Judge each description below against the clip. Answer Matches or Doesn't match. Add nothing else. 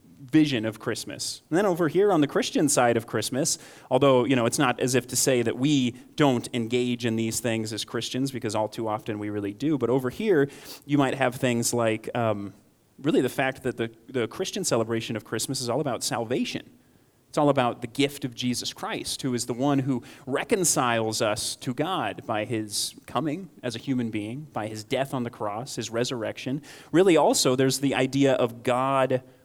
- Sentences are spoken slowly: Doesn't match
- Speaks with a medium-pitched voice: Doesn't match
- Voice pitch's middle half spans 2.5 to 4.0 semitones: Matches